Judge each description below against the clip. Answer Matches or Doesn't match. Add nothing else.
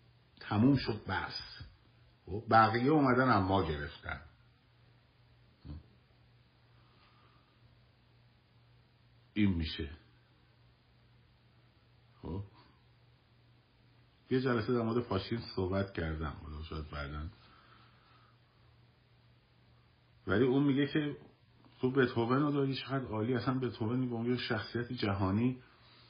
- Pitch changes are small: Matches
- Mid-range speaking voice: Doesn't match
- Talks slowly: Matches